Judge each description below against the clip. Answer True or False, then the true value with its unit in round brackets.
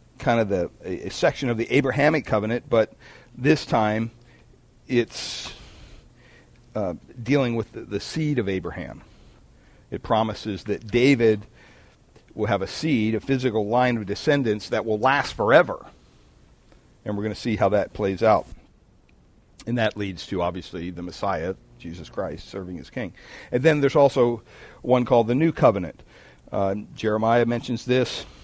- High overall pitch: False (115 Hz)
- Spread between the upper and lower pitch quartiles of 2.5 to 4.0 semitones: True (3.7 semitones)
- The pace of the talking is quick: False (150 wpm)